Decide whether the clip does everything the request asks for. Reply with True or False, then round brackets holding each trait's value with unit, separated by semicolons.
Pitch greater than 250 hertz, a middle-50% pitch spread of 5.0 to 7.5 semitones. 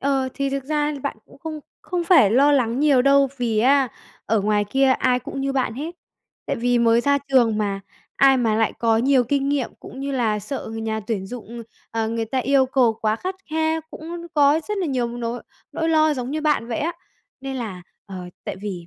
False (260 Hz; 3.8 semitones)